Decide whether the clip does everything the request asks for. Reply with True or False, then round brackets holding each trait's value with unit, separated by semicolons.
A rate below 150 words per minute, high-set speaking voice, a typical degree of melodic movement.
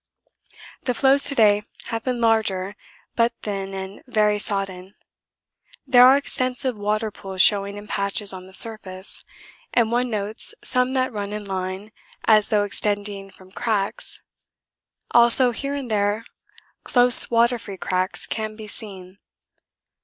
True (140 wpm; 210 Hz; 3.2 semitones)